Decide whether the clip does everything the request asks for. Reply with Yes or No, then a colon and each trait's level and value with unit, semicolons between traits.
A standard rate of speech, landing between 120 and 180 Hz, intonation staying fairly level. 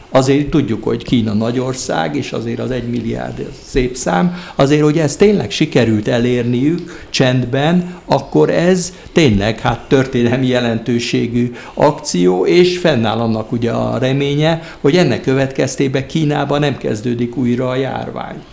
No: average, 135 wpm; low, 130 Hz; average, 3.7 semitones